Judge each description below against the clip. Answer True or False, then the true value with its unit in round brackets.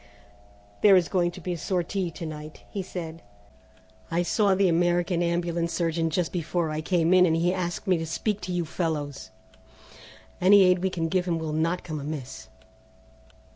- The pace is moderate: True (180 wpm)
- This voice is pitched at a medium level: True (175 Hz)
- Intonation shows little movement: True (1.9 semitones)